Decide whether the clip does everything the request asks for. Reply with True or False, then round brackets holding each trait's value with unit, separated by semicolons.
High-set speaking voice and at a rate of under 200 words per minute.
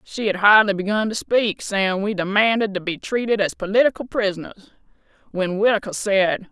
True (205 Hz; 165 wpm)